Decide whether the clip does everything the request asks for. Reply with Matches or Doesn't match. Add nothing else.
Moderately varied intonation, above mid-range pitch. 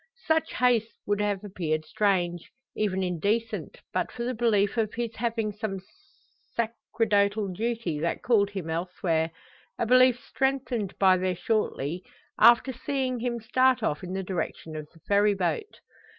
Matches